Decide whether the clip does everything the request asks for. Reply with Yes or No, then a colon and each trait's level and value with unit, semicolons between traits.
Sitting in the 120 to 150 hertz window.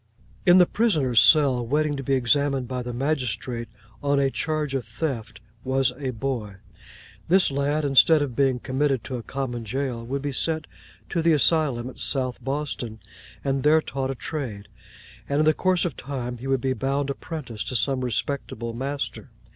Yes: low, 135 Hz